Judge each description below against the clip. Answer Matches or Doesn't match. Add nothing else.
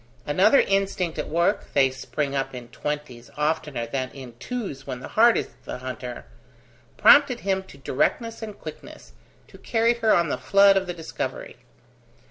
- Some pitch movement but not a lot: Doesn't match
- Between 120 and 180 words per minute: Matches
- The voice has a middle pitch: Matches